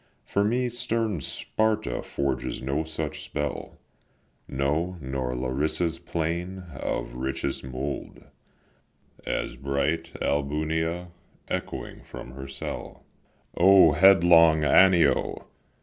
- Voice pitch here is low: Yes, very low, 80 Hz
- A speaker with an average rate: No, slow, 95 wpm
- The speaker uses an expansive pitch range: No, average, 4.4 semitones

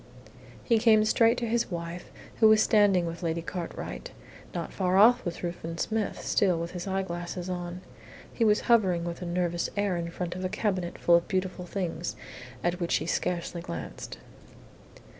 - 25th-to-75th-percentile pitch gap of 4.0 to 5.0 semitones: No, average, 3.1 semitones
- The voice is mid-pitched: Yes, medium, 180 Hz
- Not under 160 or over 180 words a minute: Yes, average, 175 wpm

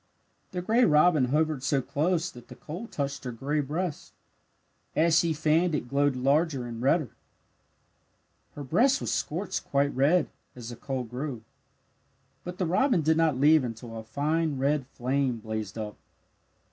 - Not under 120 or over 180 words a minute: Yes, average, 160 wpm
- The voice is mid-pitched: Yes, medium, 145 Hz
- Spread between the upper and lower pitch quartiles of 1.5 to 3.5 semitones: No, average, 4.3 semitones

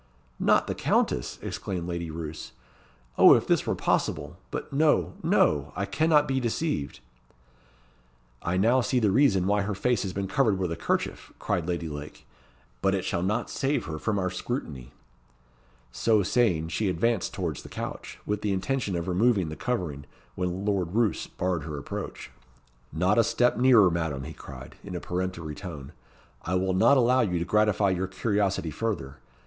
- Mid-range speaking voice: No, very low, 95 Hz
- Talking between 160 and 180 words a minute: Yes, average, 175 wpm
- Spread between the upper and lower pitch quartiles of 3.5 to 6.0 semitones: Yes, average, 4.8 semitones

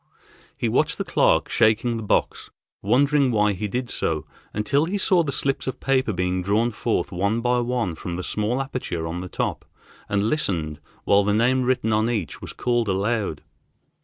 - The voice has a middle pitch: No, low, 110 Hz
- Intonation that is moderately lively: Yes, average, 4.3 semitones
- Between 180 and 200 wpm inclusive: Yes, average, 185 wpm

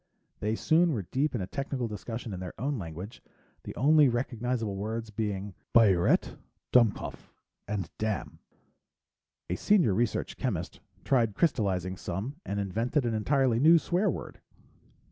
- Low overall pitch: Yes, low, 115 Hz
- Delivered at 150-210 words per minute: No, average, 140 wpm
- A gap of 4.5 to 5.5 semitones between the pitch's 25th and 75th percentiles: Yes, average, 4.8 semitones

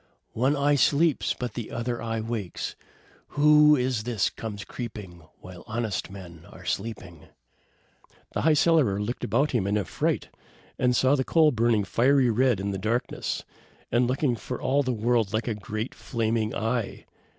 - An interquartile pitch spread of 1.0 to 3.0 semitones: No, average, 3.8 semitones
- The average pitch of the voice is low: Yes, low, 115 Hz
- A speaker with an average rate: Yes, average, 160 wpm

